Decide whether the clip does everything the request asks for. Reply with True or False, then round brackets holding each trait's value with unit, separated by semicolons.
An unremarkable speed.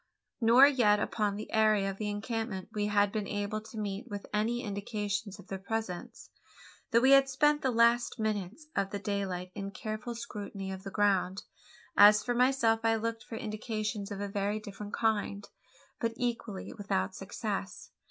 True (170 wpm)